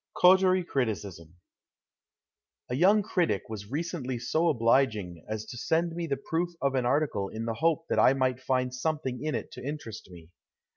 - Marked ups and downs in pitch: Yes, wide, 6.4 semitones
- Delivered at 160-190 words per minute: Yes, average, 180 wpm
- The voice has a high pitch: No, low, 130 Hz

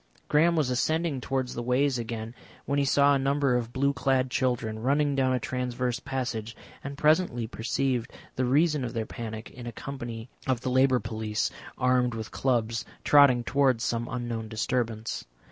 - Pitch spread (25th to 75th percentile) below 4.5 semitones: Yes, average, 2.8 semitones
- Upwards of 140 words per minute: Yes, average, 170 wpm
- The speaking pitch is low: Yes, low, 125 Hz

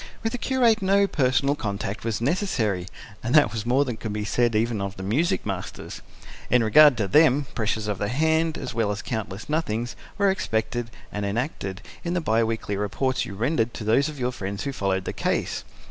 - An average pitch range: No, wide, 6.1 semitones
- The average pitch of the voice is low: Yes, low, 115 Hz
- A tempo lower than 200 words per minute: No, fast, 205 wpm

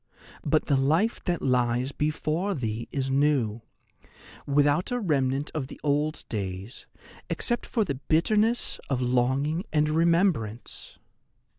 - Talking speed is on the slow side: Yes, slow, 125 wpm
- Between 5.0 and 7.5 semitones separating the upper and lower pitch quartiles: No, average, 4.4 semitones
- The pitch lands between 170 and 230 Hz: No, medium, 145 Hz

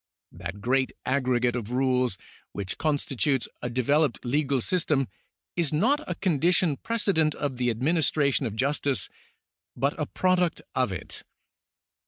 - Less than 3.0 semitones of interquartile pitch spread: No, average, 3.9 semitones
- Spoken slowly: Yes, slow, 130 wpm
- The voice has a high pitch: No, low, 135 Hz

